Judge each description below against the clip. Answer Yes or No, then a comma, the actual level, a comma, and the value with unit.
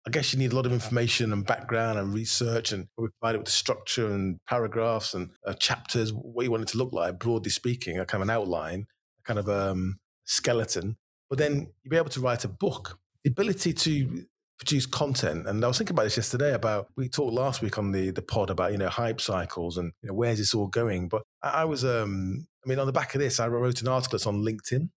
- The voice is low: Yes, low, 115 Hz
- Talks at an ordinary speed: No, fast, 255 wpm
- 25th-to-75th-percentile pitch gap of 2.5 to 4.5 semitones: Yes, average, 4.0 semitones